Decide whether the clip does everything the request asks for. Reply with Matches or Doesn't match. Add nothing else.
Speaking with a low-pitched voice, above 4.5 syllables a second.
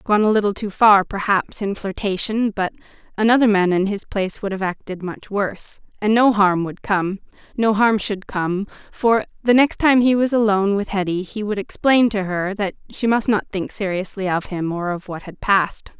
Doesn't match